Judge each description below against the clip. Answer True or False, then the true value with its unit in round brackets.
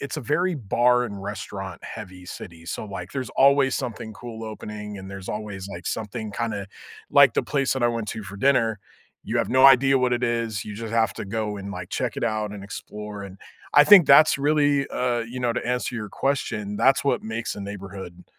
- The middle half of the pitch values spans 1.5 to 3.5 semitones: False (4.1 semitones)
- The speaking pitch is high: False (110 Hz)